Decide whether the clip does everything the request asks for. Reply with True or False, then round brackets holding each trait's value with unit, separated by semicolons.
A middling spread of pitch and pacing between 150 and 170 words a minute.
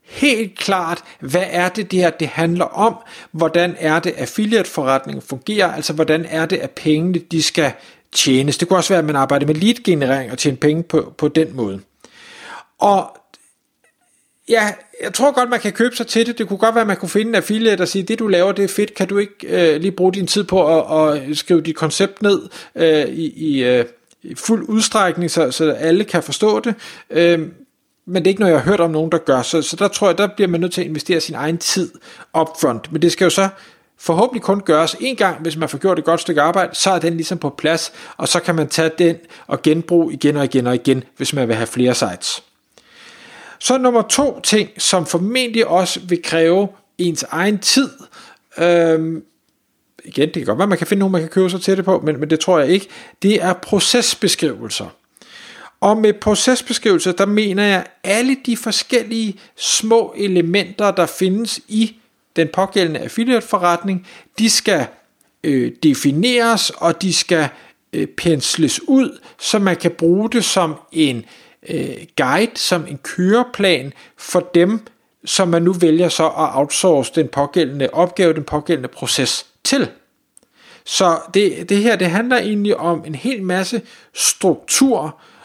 False (4.6 semitones; 195 wpm)